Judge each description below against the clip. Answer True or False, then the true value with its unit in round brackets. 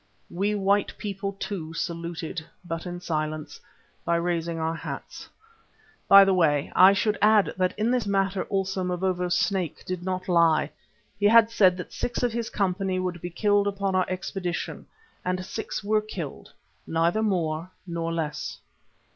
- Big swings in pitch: False (2.8 semitones)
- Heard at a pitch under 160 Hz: False (185 Hz)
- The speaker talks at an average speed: True (155 wpm)